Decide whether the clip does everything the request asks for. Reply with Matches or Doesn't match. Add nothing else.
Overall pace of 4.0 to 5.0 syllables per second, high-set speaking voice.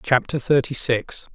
Doesn't match